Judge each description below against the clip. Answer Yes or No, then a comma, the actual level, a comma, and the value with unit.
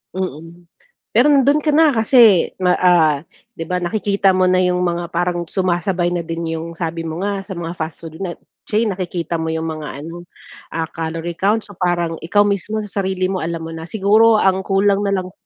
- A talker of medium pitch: Yes, medium, 180 Hz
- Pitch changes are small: No, average, 3.0 semitones